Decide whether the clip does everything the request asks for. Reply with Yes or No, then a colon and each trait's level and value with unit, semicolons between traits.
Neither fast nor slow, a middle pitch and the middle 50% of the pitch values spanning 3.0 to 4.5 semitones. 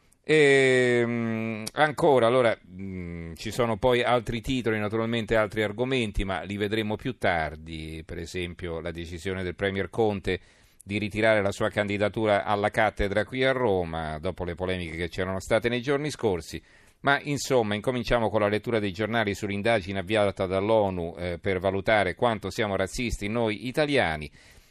No: average, 155 wpm; low, 105 Hz; average, 3.6 semitones